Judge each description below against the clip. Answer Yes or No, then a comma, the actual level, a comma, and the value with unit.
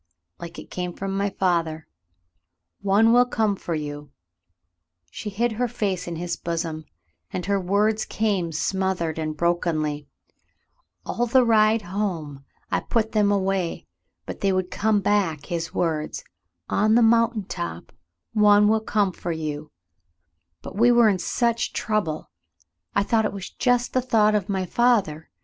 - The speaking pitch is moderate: No, high, 195 Hz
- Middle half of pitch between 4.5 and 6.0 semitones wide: Yes, average, 4.9 semitones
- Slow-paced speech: No, average, 160 wpm